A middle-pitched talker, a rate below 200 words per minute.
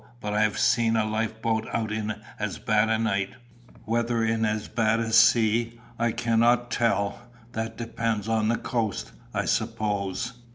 No: low, 110 Hz; average, 165 wpm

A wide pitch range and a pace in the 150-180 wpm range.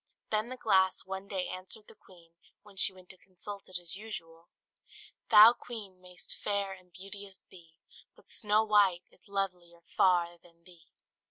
No: narrow, 2.5 semitones; average, 165 wpm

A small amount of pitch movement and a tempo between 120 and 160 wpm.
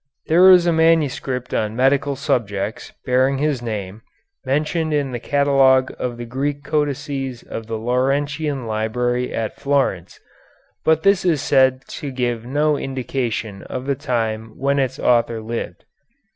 No: average, 3.4 semitones; average, 145 wpm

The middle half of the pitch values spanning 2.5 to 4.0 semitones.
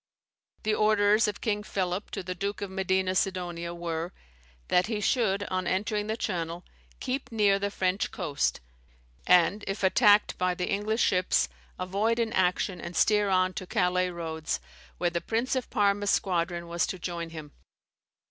Yes: average, 2.8 semitones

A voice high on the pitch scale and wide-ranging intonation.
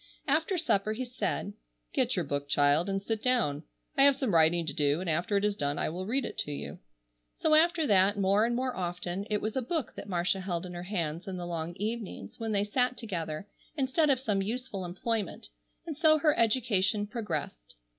Yes: high, 205 Hz; wide, 6.3 semitones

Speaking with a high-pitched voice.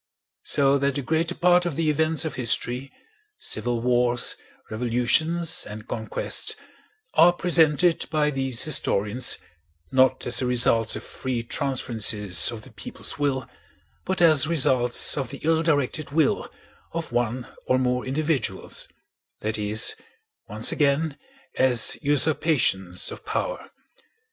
No: low, 135 Hz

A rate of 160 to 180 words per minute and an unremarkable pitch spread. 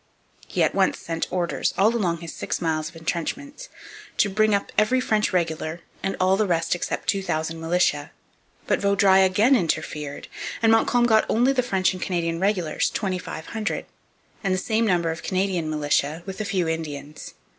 Yes: average, 170 wpm; average, 4.4 semitones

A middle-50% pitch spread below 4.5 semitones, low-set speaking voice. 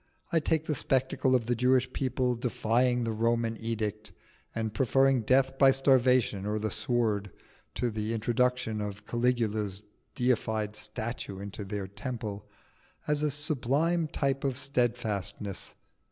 Yes: average, 3.5 semitones; low, 120 Hz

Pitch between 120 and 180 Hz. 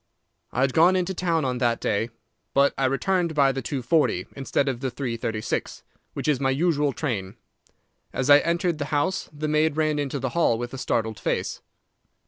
Yes: medium, 140 Hz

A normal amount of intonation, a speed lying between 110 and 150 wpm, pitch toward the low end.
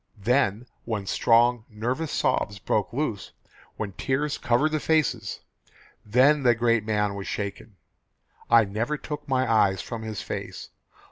Yes: average, 4.1 semitones; average, 140 wpm; low, 115 Hz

